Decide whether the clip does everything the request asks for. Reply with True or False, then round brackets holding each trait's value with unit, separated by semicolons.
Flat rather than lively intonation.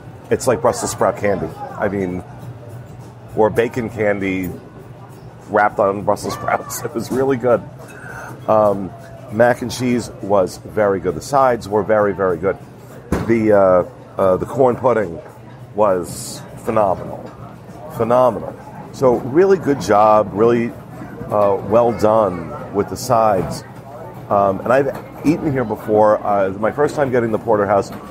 False (3.6 semitones)